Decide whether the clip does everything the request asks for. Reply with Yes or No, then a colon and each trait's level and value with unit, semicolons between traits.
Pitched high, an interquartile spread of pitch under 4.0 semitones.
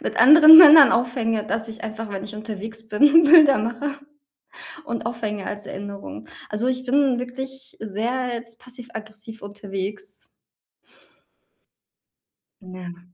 Yes: high, 225 Hz; average, 3.6 semitones